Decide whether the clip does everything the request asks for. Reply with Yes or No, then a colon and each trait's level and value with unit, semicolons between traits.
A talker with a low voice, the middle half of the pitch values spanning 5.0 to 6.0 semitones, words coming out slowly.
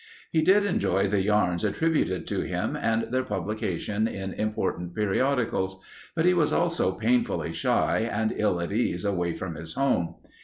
No: low, 105 Hz; average, 5.3 semitones; average, 160 wpm